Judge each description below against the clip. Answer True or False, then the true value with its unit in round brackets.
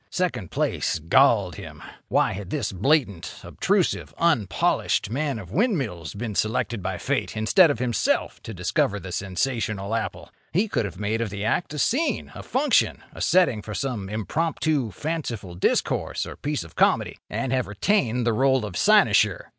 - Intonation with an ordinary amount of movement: False (6.7 semitones)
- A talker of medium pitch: False (115 Hz)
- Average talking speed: True (160 wpm)